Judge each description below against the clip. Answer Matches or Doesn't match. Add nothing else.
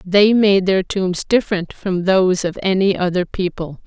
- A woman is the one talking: Matches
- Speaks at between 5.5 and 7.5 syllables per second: Doesn't match